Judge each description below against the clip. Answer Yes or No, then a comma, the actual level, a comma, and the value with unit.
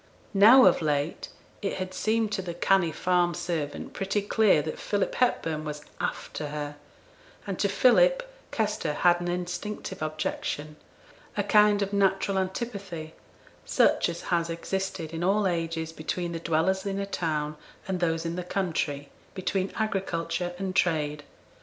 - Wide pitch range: No, average, 3.5 semitones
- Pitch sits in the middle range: Yes, medium, 180 Hz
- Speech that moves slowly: No, average, 150 wpm